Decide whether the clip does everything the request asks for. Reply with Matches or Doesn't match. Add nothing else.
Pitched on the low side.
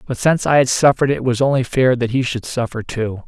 Matches